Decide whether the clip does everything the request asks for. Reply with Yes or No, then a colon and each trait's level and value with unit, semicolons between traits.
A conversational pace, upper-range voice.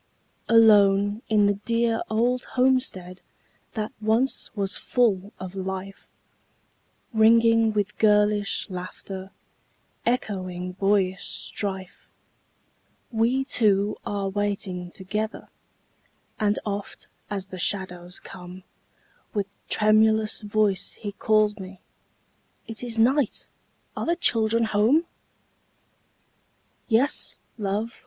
No: slow, 95 wpm; high, 210 Hz